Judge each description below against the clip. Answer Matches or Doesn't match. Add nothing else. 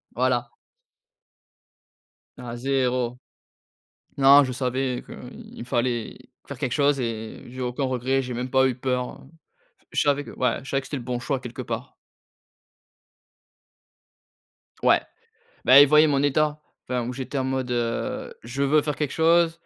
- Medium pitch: Doesn't match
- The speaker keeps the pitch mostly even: Matches